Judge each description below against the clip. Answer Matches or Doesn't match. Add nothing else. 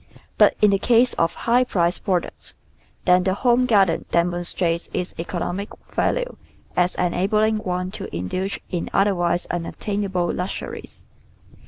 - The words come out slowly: Matches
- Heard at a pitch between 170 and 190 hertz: Matches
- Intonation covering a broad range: Doesn't match